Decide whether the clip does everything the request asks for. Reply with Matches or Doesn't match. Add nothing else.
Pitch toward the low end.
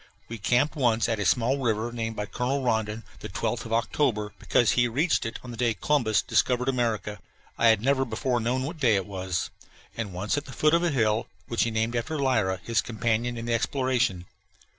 Matches